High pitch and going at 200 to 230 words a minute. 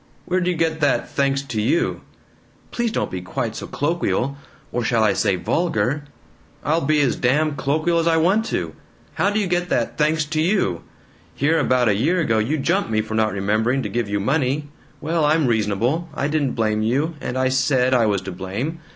No: medium, 140 Hz; fast, 205 wpm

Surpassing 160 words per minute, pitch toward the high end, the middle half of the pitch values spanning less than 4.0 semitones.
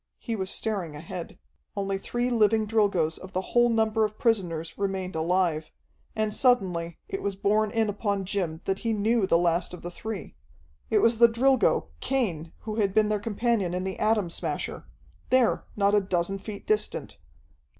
Yes: average, 175 wpm; high, 200 Hz; average, 3.5 semitones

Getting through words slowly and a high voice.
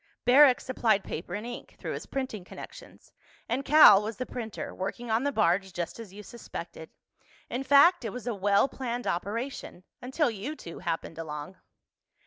No: average, 165 wpm; high, 230 Hz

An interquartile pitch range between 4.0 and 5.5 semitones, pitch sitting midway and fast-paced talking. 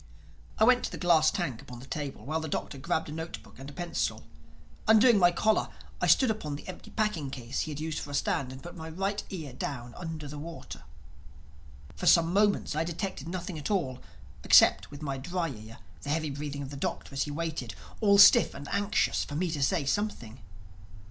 Yes: average, 4.5 semitones; medium, 155 Hz; fast, 215 wpm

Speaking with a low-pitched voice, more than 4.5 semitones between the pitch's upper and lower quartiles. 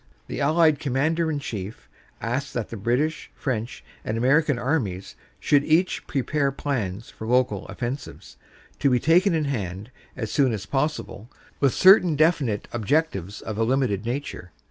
Yes: low, 130 Hz; average, 5.1 semitones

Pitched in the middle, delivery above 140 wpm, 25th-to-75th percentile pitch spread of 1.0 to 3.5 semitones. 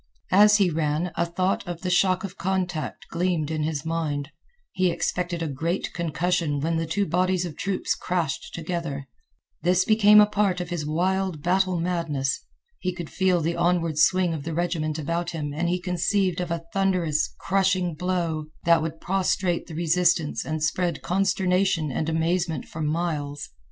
Yes: medium, 170 Hz; average, 170 wpm; narrow, 2.4 semitones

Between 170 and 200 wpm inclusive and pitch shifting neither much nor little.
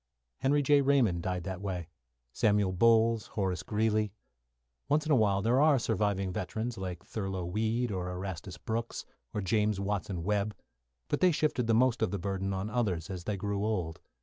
Yes: average, 175 wpm; average, 3.4 semitones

